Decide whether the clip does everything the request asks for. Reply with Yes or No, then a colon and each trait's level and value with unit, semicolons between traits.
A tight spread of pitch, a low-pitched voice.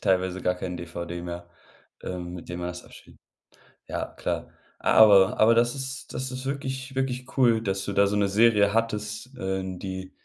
No: average, 4.7 semitones; low, 100 Hz